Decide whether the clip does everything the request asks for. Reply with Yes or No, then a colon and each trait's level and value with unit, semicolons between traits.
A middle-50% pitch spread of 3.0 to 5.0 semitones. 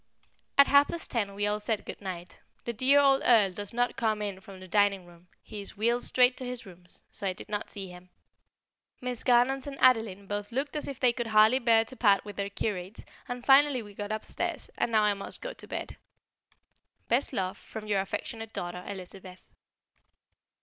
Yes: average, 3.8 semitones